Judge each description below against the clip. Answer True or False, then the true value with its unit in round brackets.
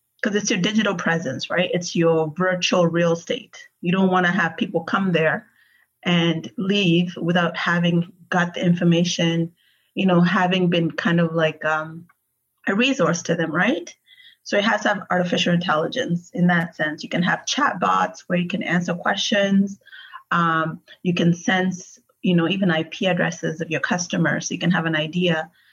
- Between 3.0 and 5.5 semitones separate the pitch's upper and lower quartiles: False (2.4 semitones)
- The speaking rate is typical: True (180 wpm)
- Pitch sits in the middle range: True (175 Hz)